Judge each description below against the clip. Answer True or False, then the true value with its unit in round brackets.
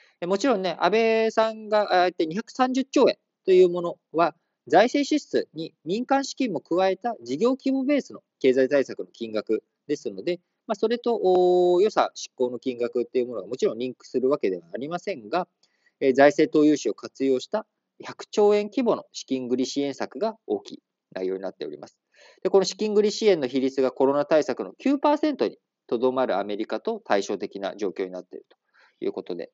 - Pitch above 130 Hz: True (185 Hz)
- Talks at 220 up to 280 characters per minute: False (345 characters per minute)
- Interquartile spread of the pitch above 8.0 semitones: True (9.0 semitones)